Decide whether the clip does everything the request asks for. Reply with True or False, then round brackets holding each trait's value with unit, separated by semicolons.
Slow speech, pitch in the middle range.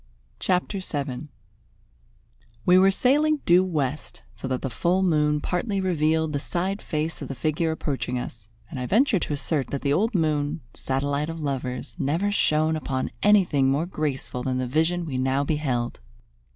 False (165 wpm; 155 Hz)